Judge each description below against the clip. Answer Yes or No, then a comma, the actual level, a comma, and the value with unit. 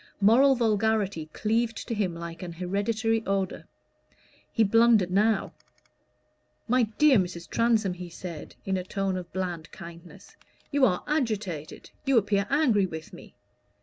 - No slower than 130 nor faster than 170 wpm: Yes, average, 140 wpm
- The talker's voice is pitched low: No, high, 200 Hz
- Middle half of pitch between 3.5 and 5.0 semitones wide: Yes, average, 4.1 semitones